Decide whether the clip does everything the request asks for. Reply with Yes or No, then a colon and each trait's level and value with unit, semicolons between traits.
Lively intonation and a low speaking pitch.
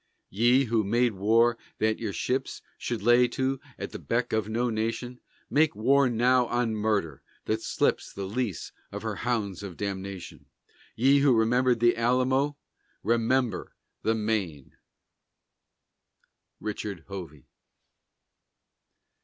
No: average, 3.2 semitones; low, 115 Hz